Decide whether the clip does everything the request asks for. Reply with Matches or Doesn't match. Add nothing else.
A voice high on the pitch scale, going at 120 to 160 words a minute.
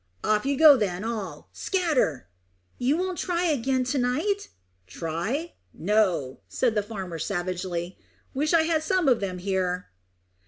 Matches